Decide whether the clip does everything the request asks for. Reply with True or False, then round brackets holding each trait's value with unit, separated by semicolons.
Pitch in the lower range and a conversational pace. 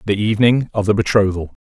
True (105 Hz; 185 wpm)